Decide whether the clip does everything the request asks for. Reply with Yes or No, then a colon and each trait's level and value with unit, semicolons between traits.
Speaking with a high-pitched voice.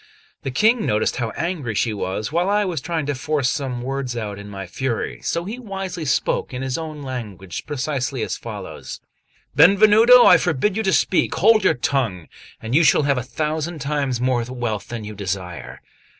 No: low, 135 Hz